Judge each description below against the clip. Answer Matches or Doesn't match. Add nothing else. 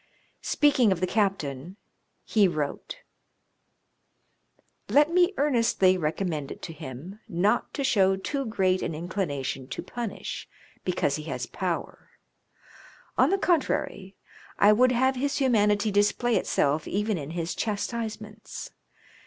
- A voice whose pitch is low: Doesn't match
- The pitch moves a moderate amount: Doesn't match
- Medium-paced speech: Doesn't match